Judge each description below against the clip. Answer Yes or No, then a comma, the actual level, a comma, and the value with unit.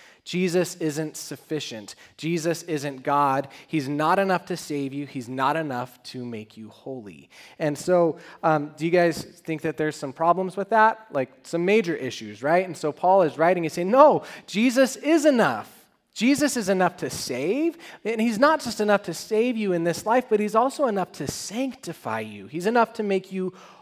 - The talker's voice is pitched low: No, medium, 170 Hz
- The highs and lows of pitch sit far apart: Yes, wide, 6.4 semitones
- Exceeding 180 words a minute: Yes, average, 190 wpm